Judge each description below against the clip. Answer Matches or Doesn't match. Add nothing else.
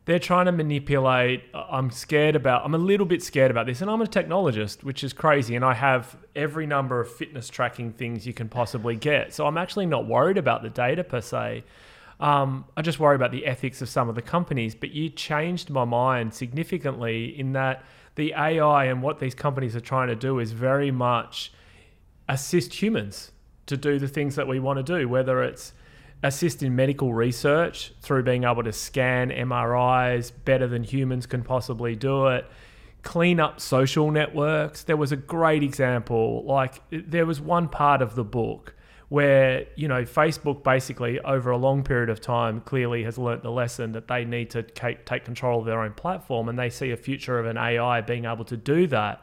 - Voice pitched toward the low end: Matches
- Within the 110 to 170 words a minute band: Doesn't match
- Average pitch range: Matches